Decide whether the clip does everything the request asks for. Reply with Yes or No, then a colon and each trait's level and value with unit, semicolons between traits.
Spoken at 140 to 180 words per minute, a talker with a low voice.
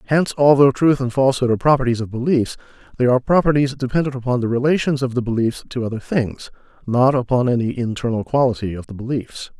No: average, 190 wpm; low, 125 Hz